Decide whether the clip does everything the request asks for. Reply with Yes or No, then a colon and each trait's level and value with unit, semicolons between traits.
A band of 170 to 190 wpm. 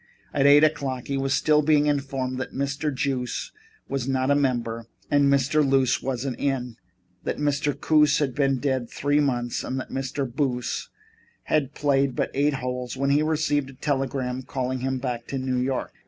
Yes: average, 180 wpm